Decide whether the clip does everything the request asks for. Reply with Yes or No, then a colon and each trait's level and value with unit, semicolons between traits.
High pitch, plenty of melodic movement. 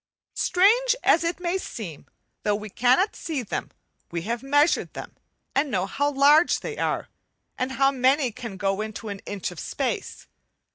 Yes: very high, 260 Hz; wide, 6.9 semitones